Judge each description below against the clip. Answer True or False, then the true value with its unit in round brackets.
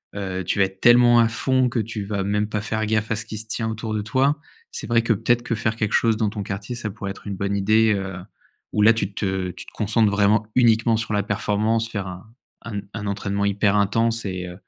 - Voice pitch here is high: False (105 Hz)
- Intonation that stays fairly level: True (2.2 semitones)